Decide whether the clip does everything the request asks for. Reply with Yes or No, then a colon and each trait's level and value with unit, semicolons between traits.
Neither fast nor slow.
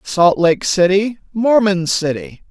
No: slow, 120 wpm